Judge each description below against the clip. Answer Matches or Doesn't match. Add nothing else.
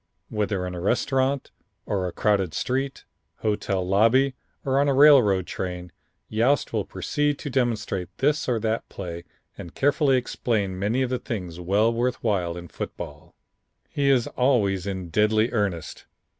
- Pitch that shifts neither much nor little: Doesn't match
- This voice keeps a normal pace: Matches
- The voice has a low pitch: Matches